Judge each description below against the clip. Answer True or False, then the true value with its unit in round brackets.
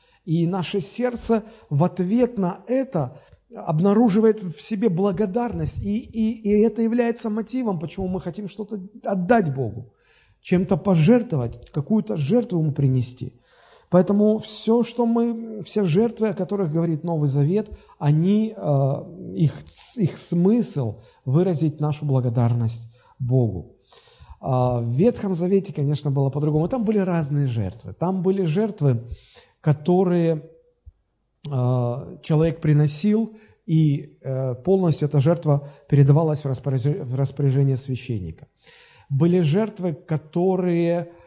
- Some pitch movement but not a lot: False (6.5 semitones)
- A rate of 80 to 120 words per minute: True (115 wpm)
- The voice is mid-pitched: True (170 Hz)